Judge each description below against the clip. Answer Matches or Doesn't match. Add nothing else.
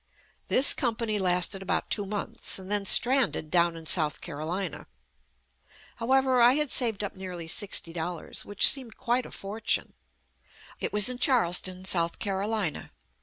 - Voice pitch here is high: Matches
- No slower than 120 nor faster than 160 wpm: Matches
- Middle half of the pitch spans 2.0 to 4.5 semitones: Doesn't match